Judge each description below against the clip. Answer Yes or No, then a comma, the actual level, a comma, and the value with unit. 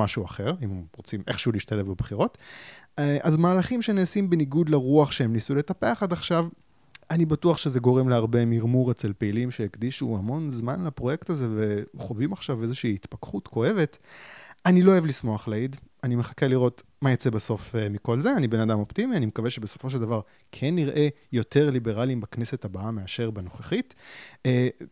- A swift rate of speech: Yes, fast, 160 wpm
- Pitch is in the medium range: No, low, 125 Hz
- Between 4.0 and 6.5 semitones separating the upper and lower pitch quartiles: Yes, average, 4.7 semitones